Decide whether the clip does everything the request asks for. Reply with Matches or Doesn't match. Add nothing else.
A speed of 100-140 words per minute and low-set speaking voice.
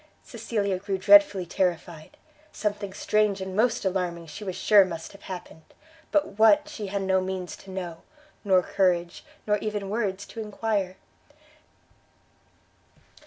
Doesn't match